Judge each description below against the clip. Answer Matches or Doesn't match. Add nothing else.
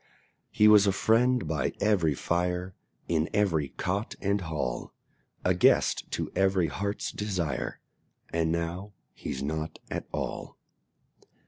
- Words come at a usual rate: Doesn't match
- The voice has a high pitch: Doesn't match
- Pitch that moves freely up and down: Doesn't match